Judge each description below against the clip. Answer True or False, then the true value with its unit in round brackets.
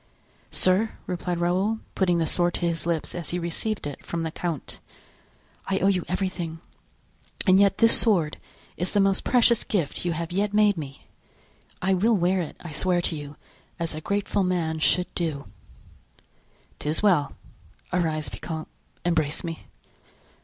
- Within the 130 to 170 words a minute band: True (160 wpm)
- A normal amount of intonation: True (3.0 semitones)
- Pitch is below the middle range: False (175 Hz)